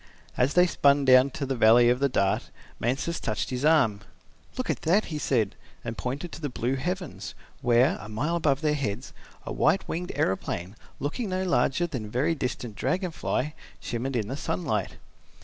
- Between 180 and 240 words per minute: Yes, average, 185 wpm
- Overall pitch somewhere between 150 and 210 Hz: No, low, 135 Hz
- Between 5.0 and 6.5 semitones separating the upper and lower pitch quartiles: Yes, average, 5.3 semitones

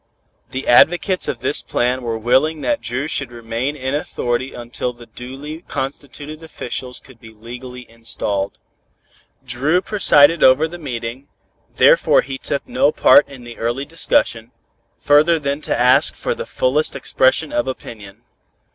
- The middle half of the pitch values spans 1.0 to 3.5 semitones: No, average, 4.2 semitones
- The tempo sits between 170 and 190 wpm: No, average, 145 wpm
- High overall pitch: No, low, 130 Hz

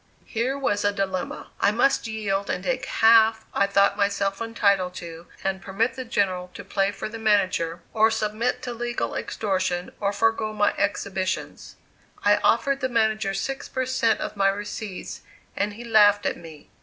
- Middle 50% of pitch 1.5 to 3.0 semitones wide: Yes, narrow, 2.6 semitones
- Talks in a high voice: Yes, high, 205 Hz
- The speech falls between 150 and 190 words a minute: Yes, average, 170 wpm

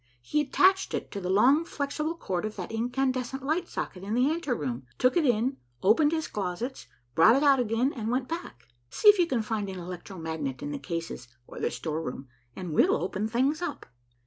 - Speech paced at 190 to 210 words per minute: Yes, average, 200 wpm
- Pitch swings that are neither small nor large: No, wide, 7.8 semitones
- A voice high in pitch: Yes, high, 230 Hz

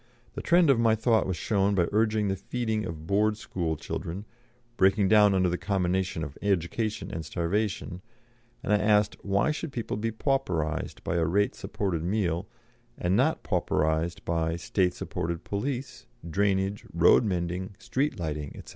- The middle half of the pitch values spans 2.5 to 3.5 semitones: No, average, 3.9 semitones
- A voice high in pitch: No, very low, 95 Hz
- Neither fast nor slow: Yes, average, 160 wpm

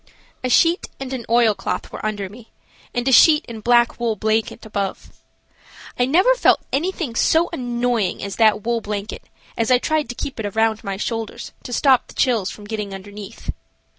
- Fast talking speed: No, average, 180 wpm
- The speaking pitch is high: Yes, high, 230 Hz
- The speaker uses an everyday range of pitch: Yes, average, 3.2 semitones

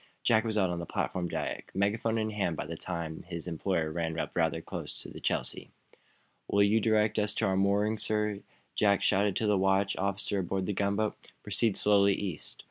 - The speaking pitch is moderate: No, low, 100 Hz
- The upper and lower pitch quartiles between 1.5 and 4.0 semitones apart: Yes, average, 2.9 semitones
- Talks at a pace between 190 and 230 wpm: Yes, fast, 205 wpm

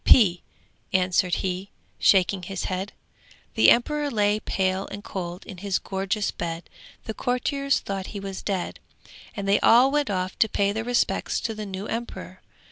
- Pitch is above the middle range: Yes, high, 200 Hz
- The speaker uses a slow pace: No, average, 165 wpm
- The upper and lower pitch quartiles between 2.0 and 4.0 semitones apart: Yes, average, 3.0 semitones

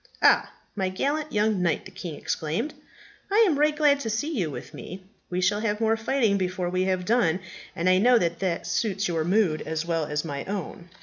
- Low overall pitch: No, high, 190 Hz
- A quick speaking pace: Yes, fast, 210 wpm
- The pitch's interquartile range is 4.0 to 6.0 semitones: Yes, average, 4.6 semitones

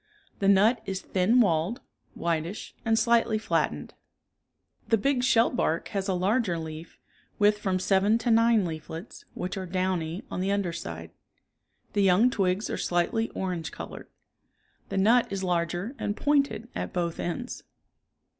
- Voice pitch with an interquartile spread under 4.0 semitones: No, average, 4.4 semitones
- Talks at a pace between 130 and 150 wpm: Yes, average, 145 wpm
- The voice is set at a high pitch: Yes, high, 195 Hz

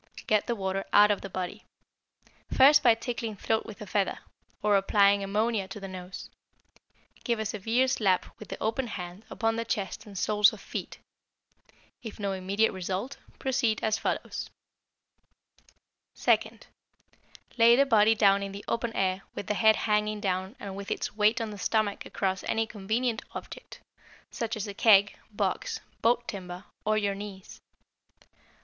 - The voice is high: Yes, high, 210 Hz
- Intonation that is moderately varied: No, narrow, 2.3 semitones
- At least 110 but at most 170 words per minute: Yes, average, 160 wpm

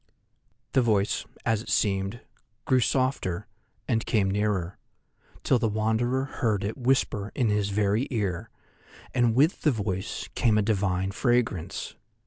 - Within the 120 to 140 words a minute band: Yes, slow, 135 wpm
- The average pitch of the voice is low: Yes, low, 110 Hz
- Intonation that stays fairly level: No, average, 3.5 semitones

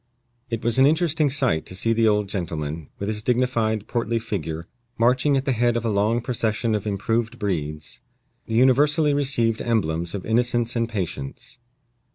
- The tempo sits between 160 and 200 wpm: Yes, average, 170 wpm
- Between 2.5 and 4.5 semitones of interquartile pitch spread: Yes, average, 3.5 semitones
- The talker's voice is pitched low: Yes, low, 115 Hz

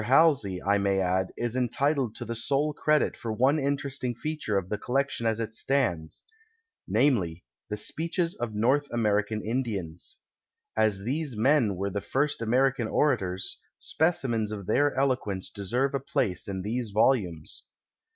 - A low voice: Yes, low, 115 Hz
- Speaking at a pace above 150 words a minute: Yes, average, 160 wpm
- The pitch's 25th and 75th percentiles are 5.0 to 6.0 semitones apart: Yes, average, 5.3 semitones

